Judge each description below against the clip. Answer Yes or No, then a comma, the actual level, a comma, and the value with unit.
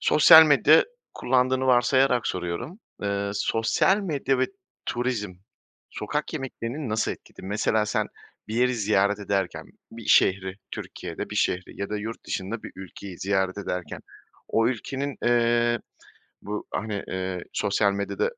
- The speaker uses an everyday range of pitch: Yes, average, 4.3 semitones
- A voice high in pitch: No, low, 110 Hz